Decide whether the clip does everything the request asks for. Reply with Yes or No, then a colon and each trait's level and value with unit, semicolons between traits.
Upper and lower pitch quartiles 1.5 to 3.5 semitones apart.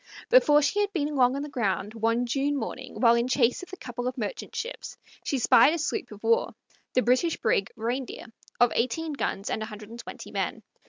No: average, 4.1 semitones